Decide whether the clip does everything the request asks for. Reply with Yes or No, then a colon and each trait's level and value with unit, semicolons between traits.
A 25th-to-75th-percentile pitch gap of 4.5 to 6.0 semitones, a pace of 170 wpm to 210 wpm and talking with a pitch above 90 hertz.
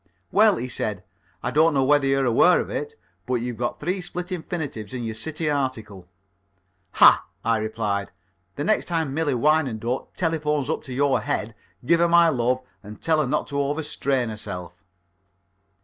Yes: wide, 5.5 semitones; average, 175 wpm; low, 135 Hz